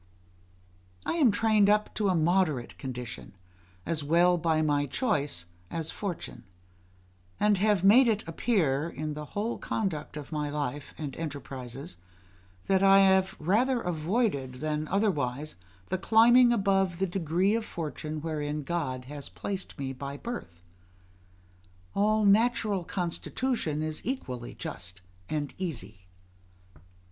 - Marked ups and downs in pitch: Yes, wide, 5.7 semitones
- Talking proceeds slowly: Yes, slow, 130 wpm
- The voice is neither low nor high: Yes, medium, 165 Hz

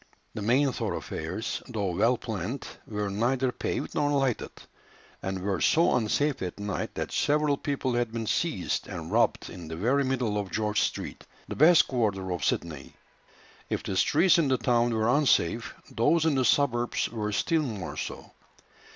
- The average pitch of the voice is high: No, low, 120 Hz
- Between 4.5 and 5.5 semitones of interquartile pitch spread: Yes, average, 5.1 semitones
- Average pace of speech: Yes, average, 170 wpm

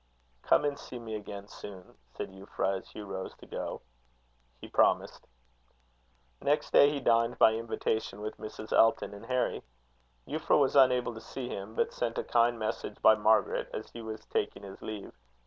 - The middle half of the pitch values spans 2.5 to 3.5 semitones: Yes, average, 3.0 semitones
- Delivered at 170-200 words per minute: Yes, average, 175 wpm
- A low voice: Yes, low, 110 Hz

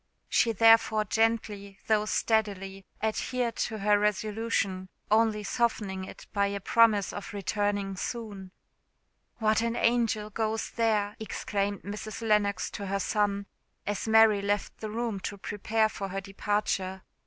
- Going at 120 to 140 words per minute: Yes, slow, 135 wpm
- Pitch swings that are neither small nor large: No, narrow, 1.8 semitones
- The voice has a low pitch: No, high, 210 Hz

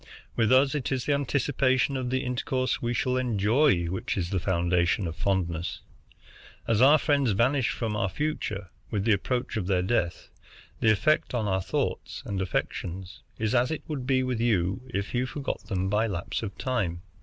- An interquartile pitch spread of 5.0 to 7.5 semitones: Yes, average, 5.3 semitones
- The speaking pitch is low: Yes, low, 115 Hz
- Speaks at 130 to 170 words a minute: No, average, 185 wpm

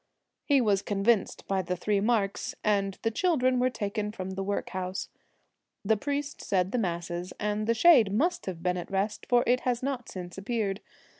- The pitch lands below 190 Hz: No, high, 205 Hz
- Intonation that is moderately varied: Yes, average, 4.1 semitones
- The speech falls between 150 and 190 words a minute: Yes, average, 180 wpm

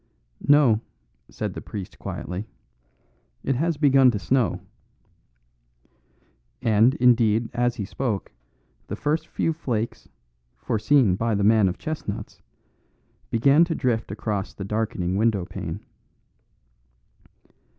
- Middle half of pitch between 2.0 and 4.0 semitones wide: No, average, 4.5 semitones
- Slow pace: Yes, slow, 110 wpm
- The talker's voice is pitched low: Yes, low, 115 Hz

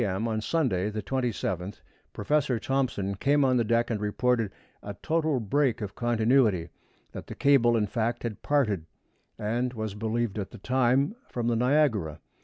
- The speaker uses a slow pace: No, average, 165 wpm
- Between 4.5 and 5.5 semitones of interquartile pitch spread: No, average, 3.7 semitones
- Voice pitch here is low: Yes, low, 115 Hz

